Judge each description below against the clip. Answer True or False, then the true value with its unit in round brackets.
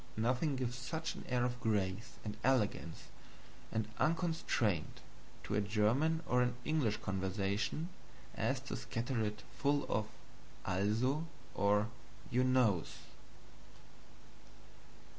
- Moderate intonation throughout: True (4.0 semitones)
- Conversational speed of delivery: False (110 wpm)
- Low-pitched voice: True (115 Hz)